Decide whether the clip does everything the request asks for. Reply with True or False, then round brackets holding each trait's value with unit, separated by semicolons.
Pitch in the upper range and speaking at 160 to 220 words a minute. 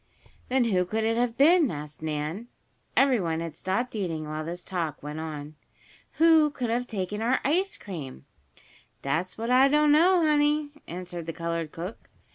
True (205 Hz; 165 wpm)